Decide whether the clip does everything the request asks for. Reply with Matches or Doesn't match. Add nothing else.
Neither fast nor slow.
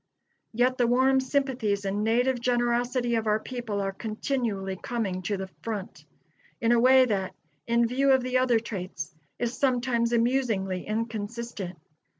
Matches